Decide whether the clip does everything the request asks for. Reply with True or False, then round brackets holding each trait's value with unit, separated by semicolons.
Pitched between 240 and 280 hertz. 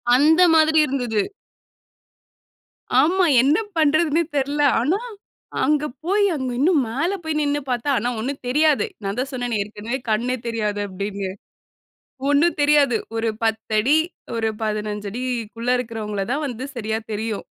True (250 Hz)